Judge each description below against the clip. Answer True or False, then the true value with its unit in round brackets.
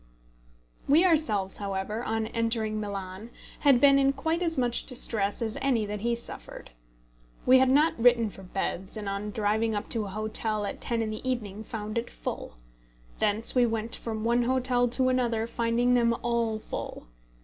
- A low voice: False (230 Hz)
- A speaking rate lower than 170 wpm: False (175 wpm)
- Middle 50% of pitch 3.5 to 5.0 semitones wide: False (2.6 semitones)